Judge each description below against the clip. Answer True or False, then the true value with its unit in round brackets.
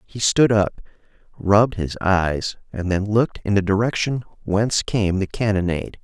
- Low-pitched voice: True (100 Hz)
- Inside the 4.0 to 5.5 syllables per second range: True (4.8 syllables/s)